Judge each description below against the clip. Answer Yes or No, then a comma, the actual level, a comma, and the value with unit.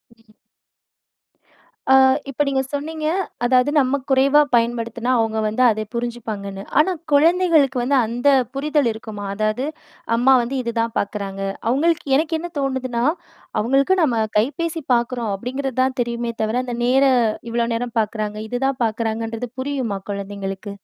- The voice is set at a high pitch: Yes, high, 240 Hz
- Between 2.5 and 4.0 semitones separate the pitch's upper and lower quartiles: Yes, average, 3.7 semitones